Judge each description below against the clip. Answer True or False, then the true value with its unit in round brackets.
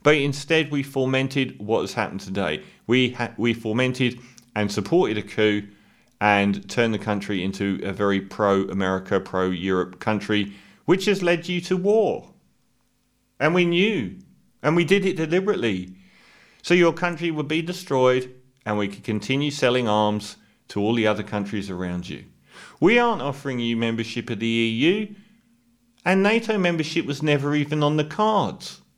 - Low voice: True (125 Hz)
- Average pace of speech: True (160 wpm)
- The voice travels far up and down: True (8.2 semitones)